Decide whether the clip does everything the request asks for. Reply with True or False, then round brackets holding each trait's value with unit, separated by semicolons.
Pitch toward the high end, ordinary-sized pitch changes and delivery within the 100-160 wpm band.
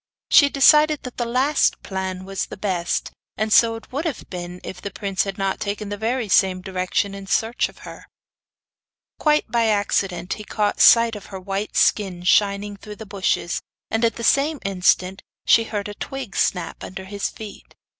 False (205 Hz; 3.2 semitones; 185 wpm)